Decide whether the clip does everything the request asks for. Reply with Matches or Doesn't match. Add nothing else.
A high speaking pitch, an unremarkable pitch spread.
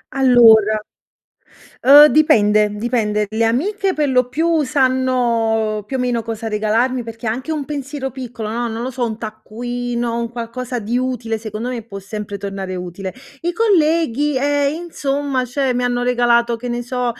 Matches